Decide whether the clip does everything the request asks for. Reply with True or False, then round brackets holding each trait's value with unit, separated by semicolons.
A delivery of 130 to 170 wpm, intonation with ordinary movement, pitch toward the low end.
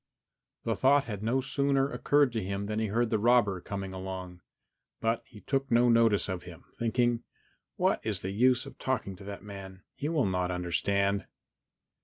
False (180 wpm; 4.2 semitones; 110 Hz)